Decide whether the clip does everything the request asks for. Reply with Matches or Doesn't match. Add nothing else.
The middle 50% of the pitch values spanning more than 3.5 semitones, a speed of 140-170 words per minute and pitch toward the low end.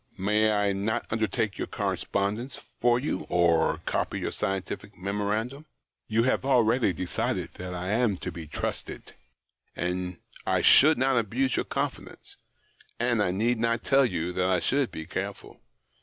Matches